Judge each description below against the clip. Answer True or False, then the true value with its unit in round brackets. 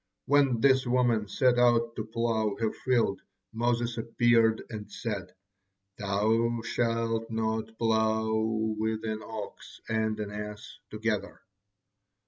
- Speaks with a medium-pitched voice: False (110 Hz)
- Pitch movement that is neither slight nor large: False (1.3 semitones)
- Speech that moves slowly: True (115 wpm)